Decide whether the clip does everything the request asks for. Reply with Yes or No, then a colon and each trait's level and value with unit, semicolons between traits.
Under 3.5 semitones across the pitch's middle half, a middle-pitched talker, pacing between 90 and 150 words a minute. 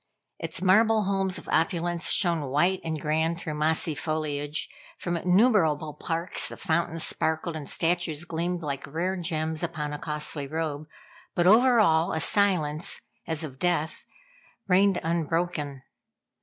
Yes: average, 2.7 semitones; medium, 165 Hz; average, 140 wpm